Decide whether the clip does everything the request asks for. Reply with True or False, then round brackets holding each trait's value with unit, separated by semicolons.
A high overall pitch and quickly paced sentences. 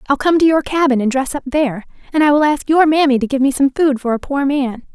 True (280 Hz; 290 wpm)